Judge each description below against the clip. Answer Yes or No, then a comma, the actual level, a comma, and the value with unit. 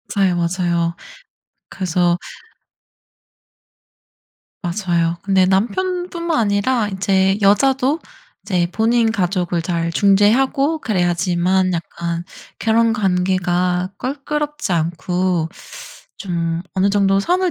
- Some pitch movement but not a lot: Yes, average, 4.3 semitones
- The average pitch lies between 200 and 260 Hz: No, high, 190 Hz